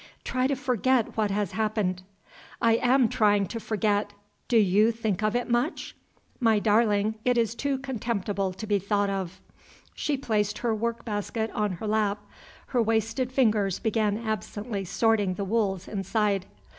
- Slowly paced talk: No, average, 155 wpm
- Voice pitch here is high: Yes, high, 215 Hz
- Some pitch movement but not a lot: No, narrow, 2.3 semitones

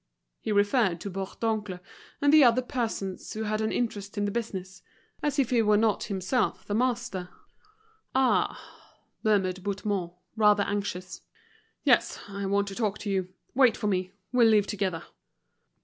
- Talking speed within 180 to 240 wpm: No, average, 155 wpm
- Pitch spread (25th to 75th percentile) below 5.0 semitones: Yes, average, 2.8 semitones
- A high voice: Yes, high, 205 Hz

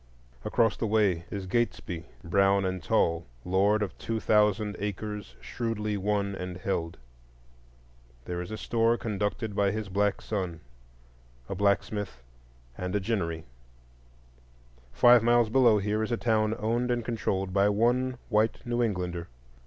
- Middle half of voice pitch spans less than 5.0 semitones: Yes, average, 2.9 semitones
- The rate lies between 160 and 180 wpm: No, average, 145 wpm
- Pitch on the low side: Yes, low, 105 Hz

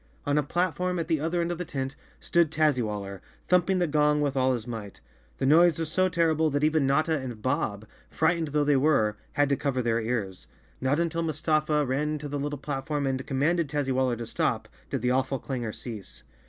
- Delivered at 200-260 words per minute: Yes, fast, 205 wpm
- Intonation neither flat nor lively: Yes, average, 3.5 semitones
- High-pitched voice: No, medium, 145 Hz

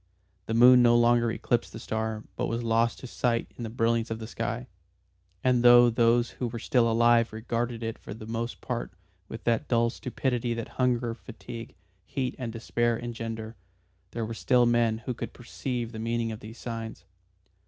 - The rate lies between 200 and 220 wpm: No, average, 185 wpm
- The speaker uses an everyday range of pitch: No, narrow, 1.1 semitones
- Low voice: Yes, low, 115 Hz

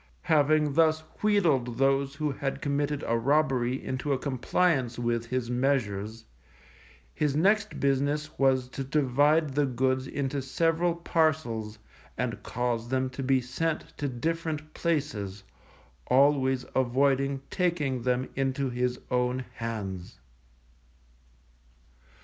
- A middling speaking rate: No, slow, 115 wpm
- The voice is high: No, low, 135 Hz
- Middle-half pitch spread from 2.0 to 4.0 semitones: Yes, average, 3.2 semitones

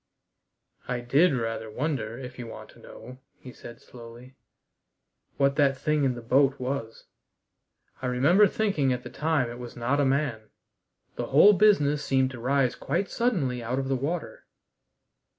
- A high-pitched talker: No, low, 135 Hz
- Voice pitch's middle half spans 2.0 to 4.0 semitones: Yes, average, 3.0 semitones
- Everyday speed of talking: Yes, average, 165 wpm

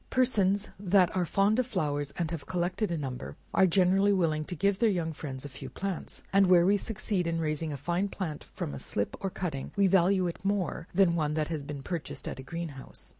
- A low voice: No, medium, 175 Hz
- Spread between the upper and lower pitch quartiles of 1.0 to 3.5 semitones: No, average, 4.2 semitones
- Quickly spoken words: Yes, fast, 225 wpm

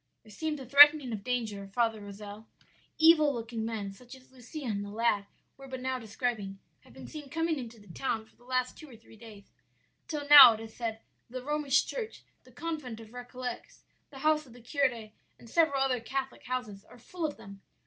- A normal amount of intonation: Yes, average, 4.1 semitones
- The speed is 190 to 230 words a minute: Yes, fast, 205 wpm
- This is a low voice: No, high, 245 Hz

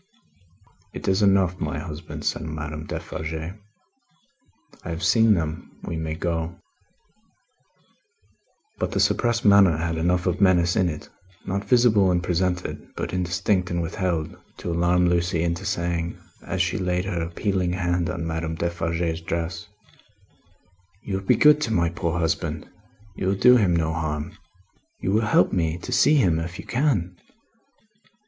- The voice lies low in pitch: Yes, very low, 85 Hz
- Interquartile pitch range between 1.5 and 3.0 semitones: Yes, narrow, 2.4 semitones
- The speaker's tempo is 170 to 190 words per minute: No, average, 155 wpm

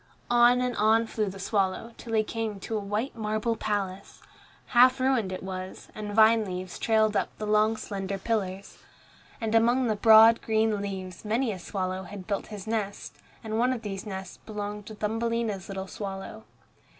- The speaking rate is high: No, average, 175 wpm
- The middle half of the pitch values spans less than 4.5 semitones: Yes, narrow, 2.5 semitones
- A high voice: Yes, high, 215 Hz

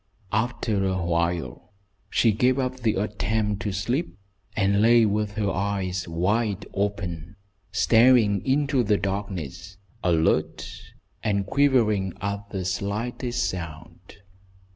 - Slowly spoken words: Yes, slow, 110 wpm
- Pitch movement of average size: Yes, average, 3.1 semitones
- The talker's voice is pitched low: Yes, low, 100 Hz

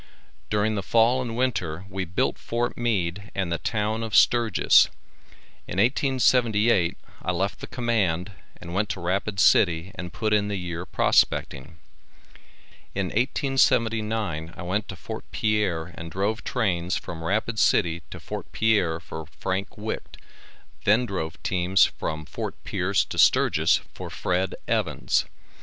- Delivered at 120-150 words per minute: Yes, average, 145 wpm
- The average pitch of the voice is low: Yes, low, 100 Hz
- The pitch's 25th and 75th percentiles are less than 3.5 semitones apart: No, average, 4.2 semitones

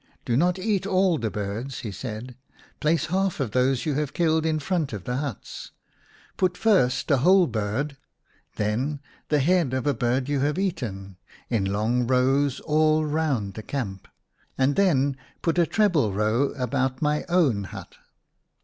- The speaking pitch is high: No, medium, 140 Hz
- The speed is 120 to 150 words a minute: No, average, 170 wpm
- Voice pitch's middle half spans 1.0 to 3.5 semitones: No, average, 5.1 semitones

